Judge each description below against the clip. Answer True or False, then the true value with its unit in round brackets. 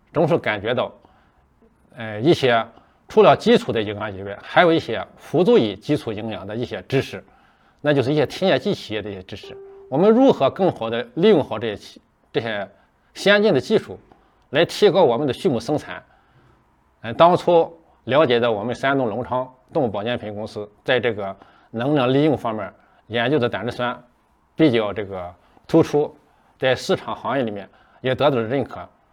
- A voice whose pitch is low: True (125 Hz)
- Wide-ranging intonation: True (5.8 semitones)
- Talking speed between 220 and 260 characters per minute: False (270 characters per minute)